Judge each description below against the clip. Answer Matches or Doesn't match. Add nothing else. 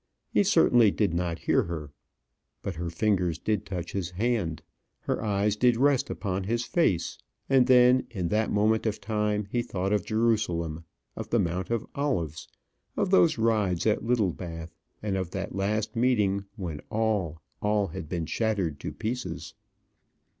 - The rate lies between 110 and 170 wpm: Matches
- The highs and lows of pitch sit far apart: Doesn't match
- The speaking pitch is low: Matches